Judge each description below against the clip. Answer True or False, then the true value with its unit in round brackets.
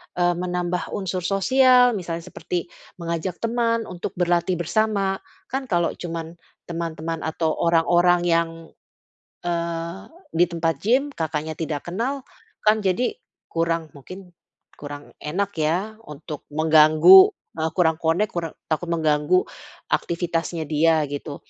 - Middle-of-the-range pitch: True (170 Hz)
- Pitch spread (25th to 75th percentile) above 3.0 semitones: False (2.6 semitones)